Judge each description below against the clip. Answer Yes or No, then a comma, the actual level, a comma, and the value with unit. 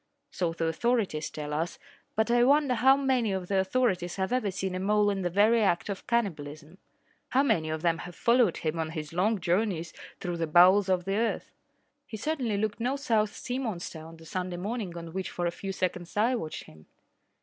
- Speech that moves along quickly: Yes, fast, 210 wpm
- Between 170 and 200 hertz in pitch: Yes, high, 190 Hz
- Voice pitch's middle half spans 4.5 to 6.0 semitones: Yes, average, 5.0 semitones